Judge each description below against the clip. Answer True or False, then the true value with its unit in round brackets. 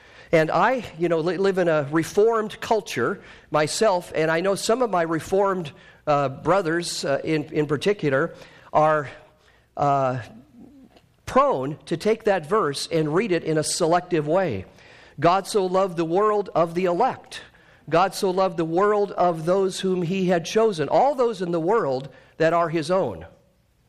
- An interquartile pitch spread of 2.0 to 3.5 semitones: False (4.2 semitones)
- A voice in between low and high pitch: True (175 Hz)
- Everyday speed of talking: True (165 wpm)